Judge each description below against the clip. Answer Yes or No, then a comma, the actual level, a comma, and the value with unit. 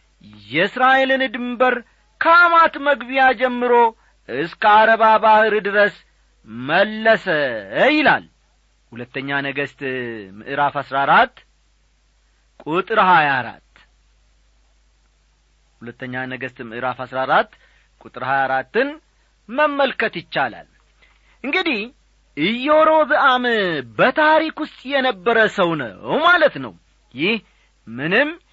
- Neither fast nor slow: Yes, average, 85 wpm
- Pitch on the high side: Yes, high, 205 Hz